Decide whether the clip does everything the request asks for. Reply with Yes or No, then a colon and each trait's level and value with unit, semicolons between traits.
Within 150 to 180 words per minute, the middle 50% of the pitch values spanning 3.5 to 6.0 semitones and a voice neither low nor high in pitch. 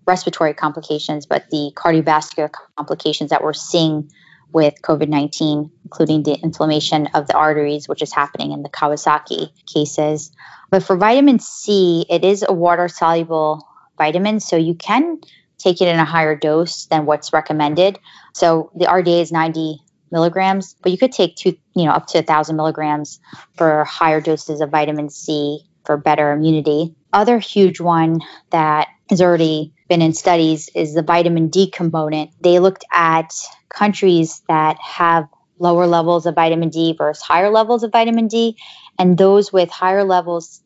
No: average, 160 wpm; average, 2.9 semitones; medium, 165 Hz